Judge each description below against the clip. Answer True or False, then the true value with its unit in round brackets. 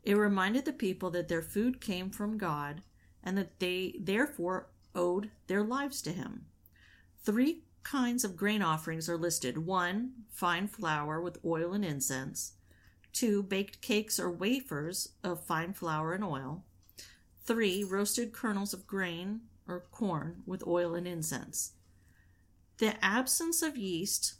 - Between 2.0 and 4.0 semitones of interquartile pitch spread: False (4.5 semitones)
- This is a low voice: False (185 Hz)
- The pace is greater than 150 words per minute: False (145 wpm)